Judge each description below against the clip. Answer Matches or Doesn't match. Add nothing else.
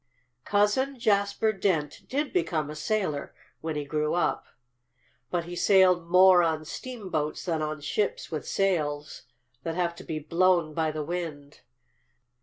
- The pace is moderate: Matches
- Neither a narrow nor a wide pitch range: Matches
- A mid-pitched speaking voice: Matches